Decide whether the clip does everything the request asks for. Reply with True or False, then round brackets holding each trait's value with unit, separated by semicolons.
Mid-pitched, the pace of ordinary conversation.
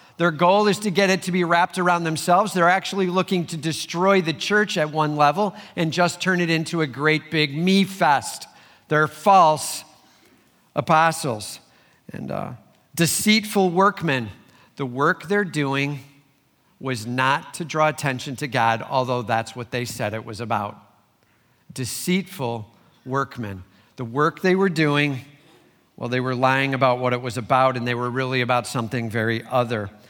True (145 Hz; 160 wpm)